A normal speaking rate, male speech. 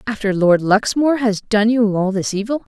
No: average, 195 wpm; female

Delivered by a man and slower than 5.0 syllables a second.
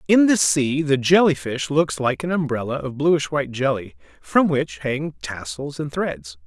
Yes: male; 4.4 syllables/s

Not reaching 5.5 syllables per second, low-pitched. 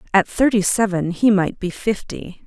No: 4.5 syllables/s; high, 200 Hz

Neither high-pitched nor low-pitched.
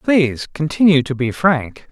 Yes: medium, 150 Hz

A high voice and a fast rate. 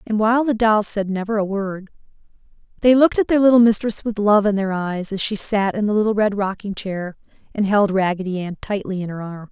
Yes: high, 205 Hz; fast, 225 wpm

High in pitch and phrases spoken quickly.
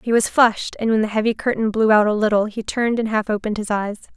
Yes: high, 215 Hz; fast, 275 wpm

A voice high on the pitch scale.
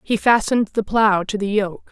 Yes: high, 210 Hz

